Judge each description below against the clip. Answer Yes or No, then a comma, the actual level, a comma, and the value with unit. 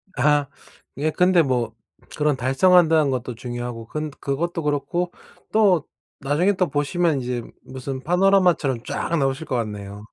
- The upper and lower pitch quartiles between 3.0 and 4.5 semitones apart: No, average, 5.3 semitones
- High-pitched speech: No, medium, 145 Hz